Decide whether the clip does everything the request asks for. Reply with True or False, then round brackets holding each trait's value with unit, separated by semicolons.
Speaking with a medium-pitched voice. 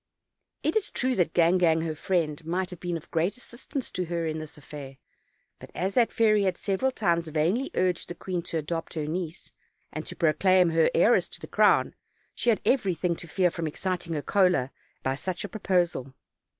True (175 Hz)